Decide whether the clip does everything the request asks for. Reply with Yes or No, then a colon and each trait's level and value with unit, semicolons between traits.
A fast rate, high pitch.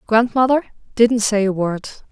No: average, 140 wpm; high, 225 Hz